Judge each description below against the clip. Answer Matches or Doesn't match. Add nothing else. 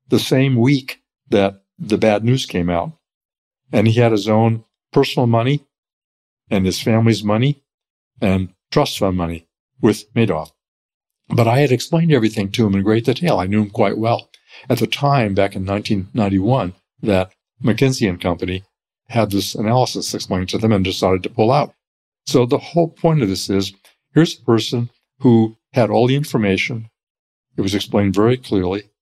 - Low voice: Matches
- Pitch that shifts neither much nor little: Matches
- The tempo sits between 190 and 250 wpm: Doesn't match